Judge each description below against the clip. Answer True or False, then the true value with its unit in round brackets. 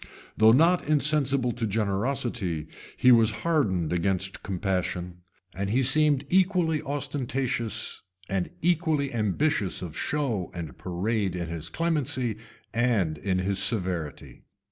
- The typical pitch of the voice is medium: False (115 Hz)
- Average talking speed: False (120 wpm)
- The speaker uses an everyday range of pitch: False (7.0 semitones)